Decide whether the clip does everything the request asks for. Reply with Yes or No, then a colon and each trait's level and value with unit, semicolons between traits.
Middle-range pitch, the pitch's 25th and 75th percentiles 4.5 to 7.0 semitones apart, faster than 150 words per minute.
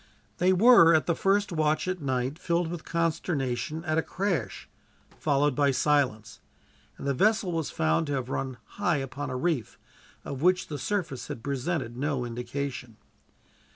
Yes: medium, 150 Hz; average, 4.8 semitones; average, 160 wpm